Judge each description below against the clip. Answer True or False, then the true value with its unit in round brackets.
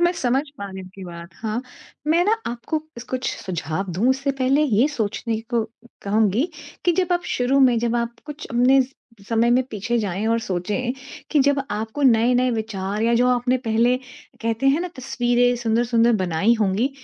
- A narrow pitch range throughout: False (3.2 semitones)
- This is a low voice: False (235 Hz)